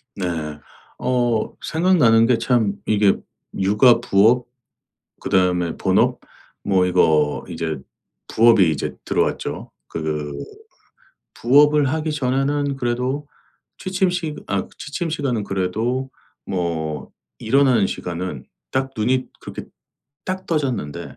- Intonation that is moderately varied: No, wide, 7.1 semitones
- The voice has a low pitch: Yes, low, 115 Hz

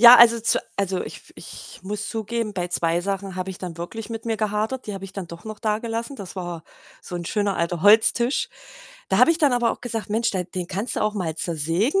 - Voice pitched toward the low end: No, high, 205 Hz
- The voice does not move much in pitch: No, average, 3.9 semitones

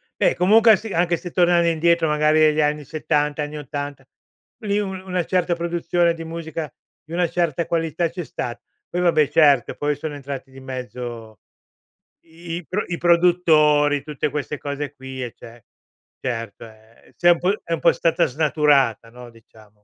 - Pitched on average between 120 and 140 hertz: No, medium, 155 Hz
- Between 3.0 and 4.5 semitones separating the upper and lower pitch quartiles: Yes, average, 3.9 semitones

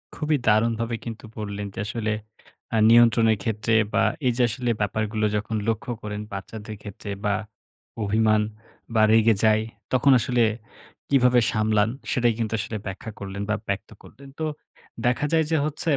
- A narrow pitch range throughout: Yes, narrow, 2.0 semitones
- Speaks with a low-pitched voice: Yes, low, 110 Hz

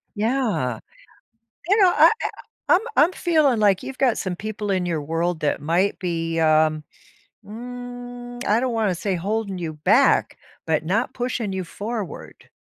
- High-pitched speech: Yes, high, 205 Hz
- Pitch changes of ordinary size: No, wide, 6.3 semitones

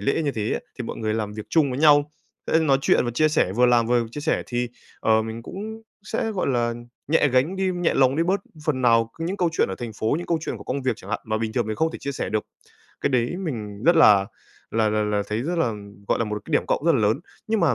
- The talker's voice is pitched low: Yes, low, 125 Hz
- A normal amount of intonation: No, wide, 6.4 semitones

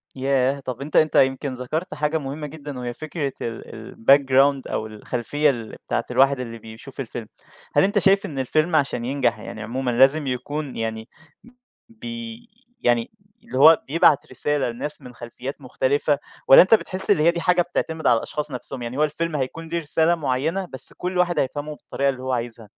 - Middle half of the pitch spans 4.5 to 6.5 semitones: No, average, 3.6 semitones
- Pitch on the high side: No, medium, 140 Hz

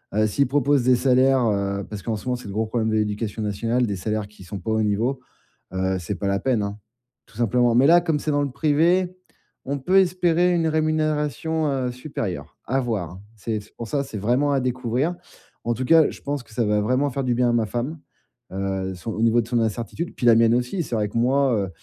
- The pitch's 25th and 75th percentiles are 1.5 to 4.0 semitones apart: No, average, 4.8 semitones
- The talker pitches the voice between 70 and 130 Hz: Yes, low, 120 Hz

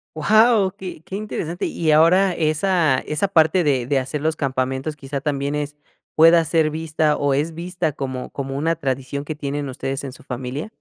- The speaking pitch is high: No, medium, 150 Hz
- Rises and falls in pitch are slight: No, average, 3.2 semitones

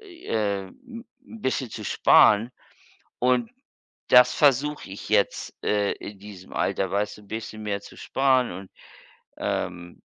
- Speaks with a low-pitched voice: Yes, low, 110 Hz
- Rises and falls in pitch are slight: No, average, 4.6 semitones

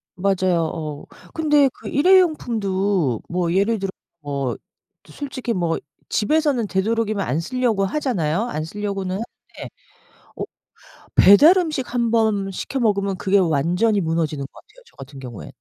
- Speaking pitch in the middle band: No, high, 200 Hz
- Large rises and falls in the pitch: Yes, wide, 6.1 semitones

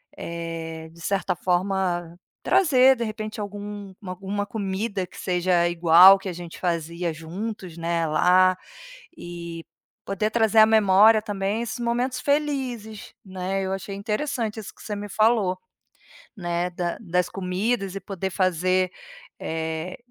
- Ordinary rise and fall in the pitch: Yes, average, 3.6 semitones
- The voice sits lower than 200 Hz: Yes, high, 190 Hz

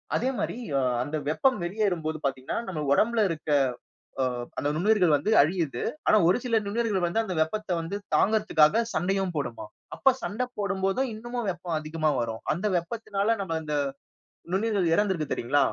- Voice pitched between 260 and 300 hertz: No, medium, 185 Hz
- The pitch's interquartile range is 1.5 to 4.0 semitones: No, wide, 5.4 semitones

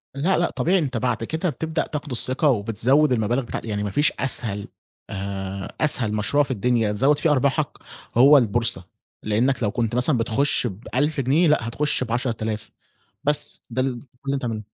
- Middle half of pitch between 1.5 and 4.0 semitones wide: No, average, 4.7 semitones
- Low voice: Yes, low, 125 Hz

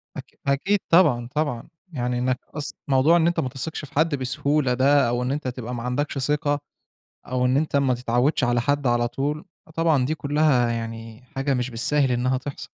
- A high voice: No, low, 135 Hz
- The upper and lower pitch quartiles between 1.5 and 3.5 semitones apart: Yes, average, 3.1 semitones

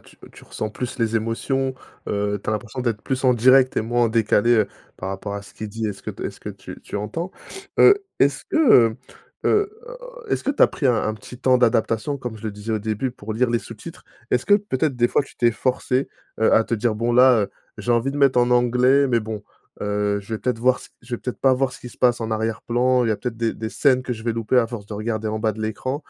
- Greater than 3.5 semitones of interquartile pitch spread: No, average, 2.8 semitones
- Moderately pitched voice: No, low, 120 Hz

